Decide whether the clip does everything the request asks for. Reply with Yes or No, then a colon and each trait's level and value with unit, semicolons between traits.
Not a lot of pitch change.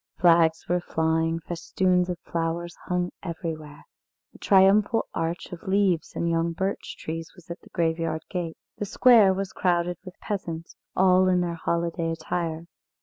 Yes: narrow, 2.1 semitones